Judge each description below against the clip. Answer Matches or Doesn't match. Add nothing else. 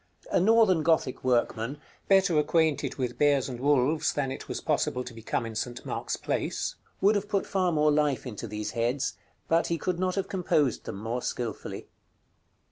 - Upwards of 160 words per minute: Matches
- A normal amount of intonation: Doesn't match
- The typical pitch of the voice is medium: Matches